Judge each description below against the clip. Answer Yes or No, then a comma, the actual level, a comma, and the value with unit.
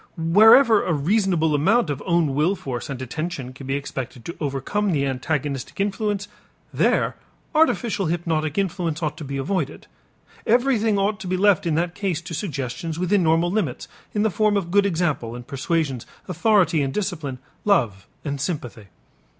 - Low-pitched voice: No, medium, 165 Hz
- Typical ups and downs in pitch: No, wide, 6.0 semitones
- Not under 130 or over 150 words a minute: No, average, 165 wpm